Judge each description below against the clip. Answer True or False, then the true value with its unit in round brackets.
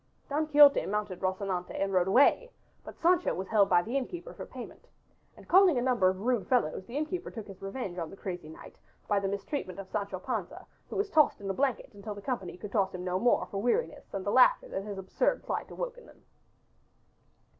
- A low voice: False (205 Hz)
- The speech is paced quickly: True (220 wpm)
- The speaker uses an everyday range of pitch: False (6.5 semitones)